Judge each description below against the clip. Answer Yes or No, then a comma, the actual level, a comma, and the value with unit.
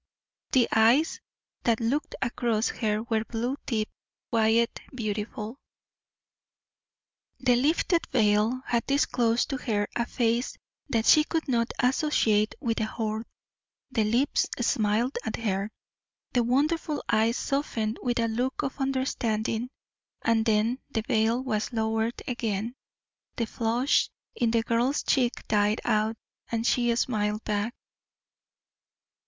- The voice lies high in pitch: Yes, high, 230 Hz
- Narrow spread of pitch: Yes, narrow, 2.3 semitones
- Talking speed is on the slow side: Yes, slow, 125 wpm